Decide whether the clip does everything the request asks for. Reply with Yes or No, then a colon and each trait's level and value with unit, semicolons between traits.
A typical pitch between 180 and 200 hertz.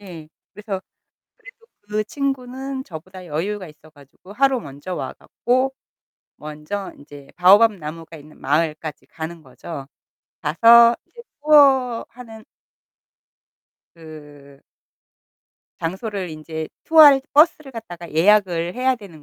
Yes: medium, 185 Hz